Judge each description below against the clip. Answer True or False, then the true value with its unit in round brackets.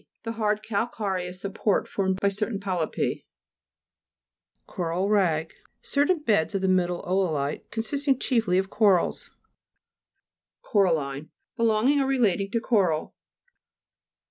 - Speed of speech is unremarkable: False (115 wpm)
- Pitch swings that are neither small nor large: True (4.0 semitones)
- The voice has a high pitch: True (200 Hz)